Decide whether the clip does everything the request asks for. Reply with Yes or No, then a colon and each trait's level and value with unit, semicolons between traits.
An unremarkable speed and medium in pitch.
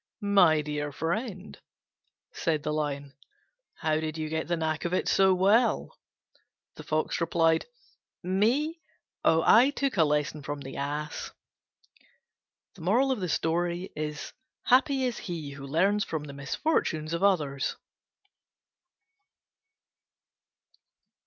No: slow, 105 wpm; medium, 165 Hz